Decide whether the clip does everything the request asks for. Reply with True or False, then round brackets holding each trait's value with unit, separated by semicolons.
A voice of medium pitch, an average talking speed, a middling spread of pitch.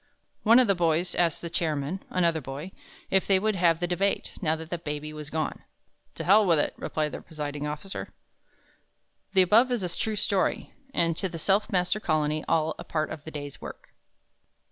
True (170 Hz; 195 wpm; 3.7 semitones)